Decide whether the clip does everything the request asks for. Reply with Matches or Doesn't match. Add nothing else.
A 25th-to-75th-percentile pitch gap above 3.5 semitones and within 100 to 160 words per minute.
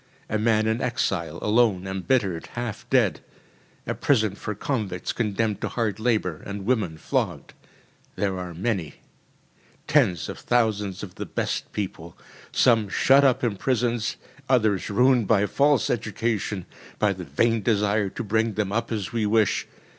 Doesn't match